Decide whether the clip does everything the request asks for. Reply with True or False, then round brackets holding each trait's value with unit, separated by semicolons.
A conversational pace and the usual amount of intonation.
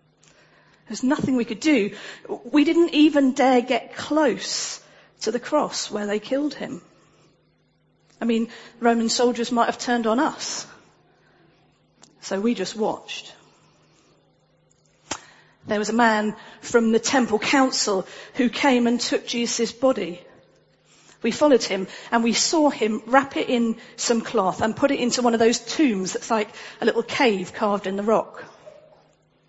True (150 wpm; 3.1 semitones)